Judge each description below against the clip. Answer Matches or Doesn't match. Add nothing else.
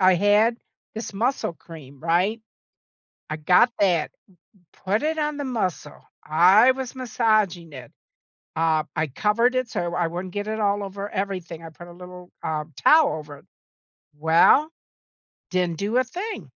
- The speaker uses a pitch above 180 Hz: Matches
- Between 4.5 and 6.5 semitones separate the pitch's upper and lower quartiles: Matches